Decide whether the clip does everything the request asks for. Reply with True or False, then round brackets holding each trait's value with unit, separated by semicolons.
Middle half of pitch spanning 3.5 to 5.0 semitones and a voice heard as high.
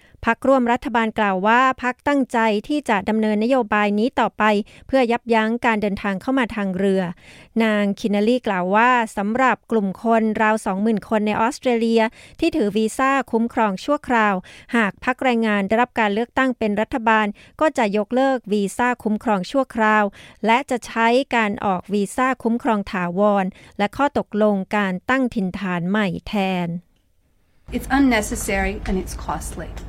False (3.0 semitones; 220 Hz)